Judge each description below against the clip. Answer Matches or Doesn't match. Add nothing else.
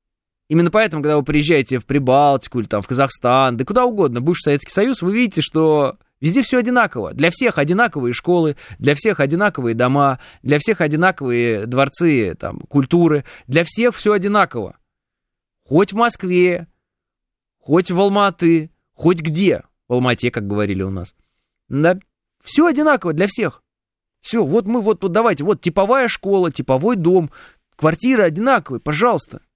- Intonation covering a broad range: Matches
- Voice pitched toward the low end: Doesn't match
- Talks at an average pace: Matches